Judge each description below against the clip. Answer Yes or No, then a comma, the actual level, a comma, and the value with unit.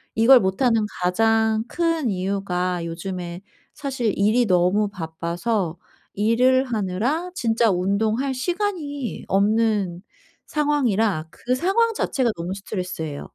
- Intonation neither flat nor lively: No, wide, 5.8 semitones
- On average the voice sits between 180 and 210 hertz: No, high, 220 Hz